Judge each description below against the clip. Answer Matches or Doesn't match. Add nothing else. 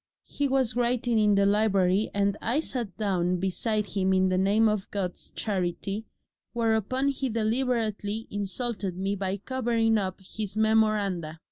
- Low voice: Doesn't match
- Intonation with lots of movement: Doesn't match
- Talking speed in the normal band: Matches